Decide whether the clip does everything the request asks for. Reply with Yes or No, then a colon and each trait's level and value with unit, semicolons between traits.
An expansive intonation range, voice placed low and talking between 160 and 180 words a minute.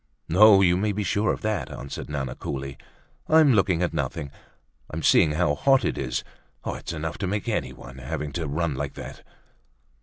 Yes: wide, 6.2 semitones; very low, 85 Hz; average, 175 wpm